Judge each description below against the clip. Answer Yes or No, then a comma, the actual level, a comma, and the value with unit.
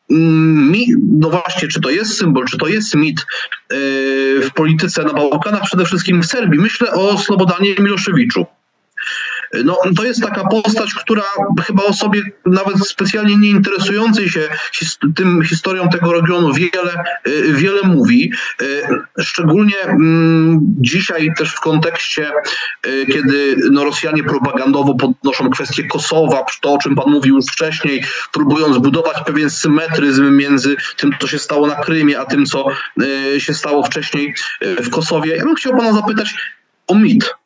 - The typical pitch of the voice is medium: Yes, medium, 165 Hz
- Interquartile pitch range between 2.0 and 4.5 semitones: No, average, 5.3 semitones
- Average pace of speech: Yes, average, 140 wpm